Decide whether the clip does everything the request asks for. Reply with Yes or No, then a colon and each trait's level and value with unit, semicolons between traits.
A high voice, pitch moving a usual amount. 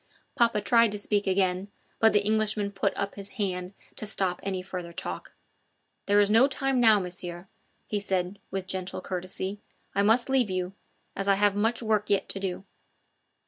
No: high, 200 Hz; narrow, 2.3 semitones